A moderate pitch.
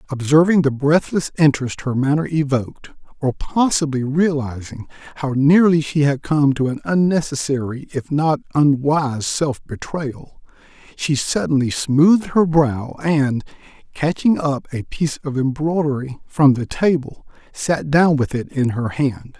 Yes: medium, 145 Hz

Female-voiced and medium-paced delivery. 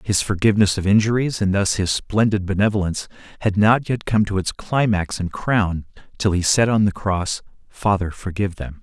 No: male; average, 185 wpm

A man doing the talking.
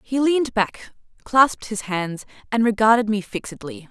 No: female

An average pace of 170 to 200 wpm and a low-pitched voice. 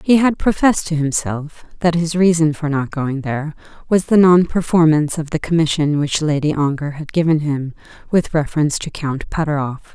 No: average, 180 wpm; medium, 155 Hz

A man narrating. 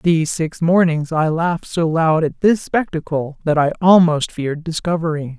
No: female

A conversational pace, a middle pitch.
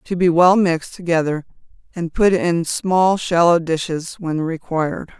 Yes: average, 150 wpm; medium, 170 Hz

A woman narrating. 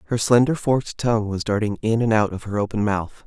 No: male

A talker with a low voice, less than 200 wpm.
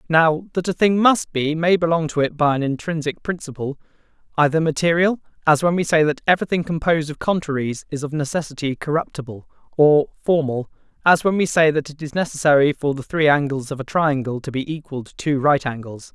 No: medium, 155 Hz; average, 190 wpm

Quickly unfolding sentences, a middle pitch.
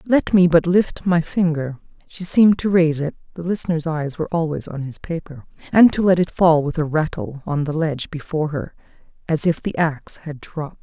Yes: fast, 210 wpm; medium, 165 Hz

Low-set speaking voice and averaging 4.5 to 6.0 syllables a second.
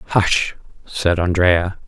No: very low, 90 Hz; 2.7 syllables/s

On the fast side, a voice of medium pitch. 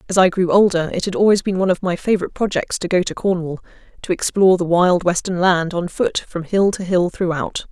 Yes: fast, 235 wpm; medium, 180 Hz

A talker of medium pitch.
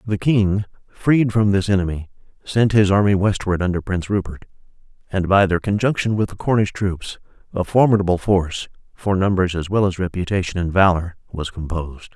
No: very low, 95 Hz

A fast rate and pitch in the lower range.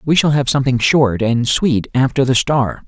Yes: fast, 210 wpm; low, 130 Hz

